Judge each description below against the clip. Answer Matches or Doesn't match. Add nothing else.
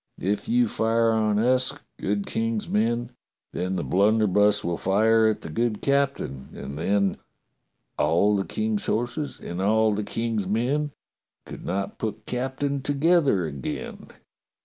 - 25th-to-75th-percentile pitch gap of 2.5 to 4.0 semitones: Matches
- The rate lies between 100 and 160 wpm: Matches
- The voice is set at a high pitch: Doesn't match